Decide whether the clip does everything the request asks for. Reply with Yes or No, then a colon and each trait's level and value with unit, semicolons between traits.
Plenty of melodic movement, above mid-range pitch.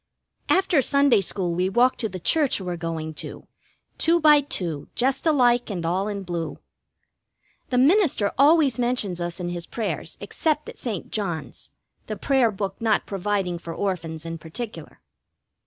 Yes: wide, 7.0 semitones; high, 205 Hz